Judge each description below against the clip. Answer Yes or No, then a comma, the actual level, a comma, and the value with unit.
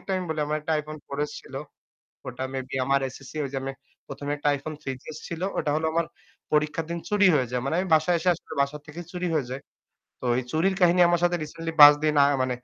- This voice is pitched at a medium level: Yes, medium, 150 Hz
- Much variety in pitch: No, average, 3.5 semitones